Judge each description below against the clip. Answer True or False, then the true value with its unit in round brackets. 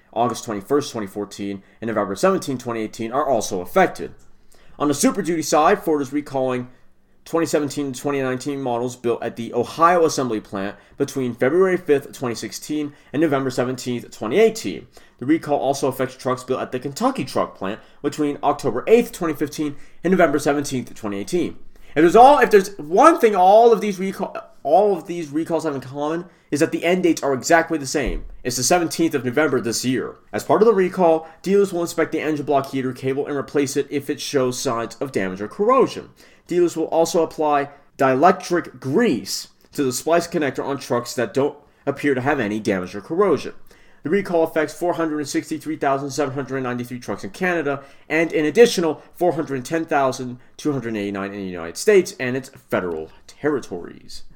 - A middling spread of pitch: True (4.6 semitones)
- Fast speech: False (170 wpm)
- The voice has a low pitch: False (145 Hz)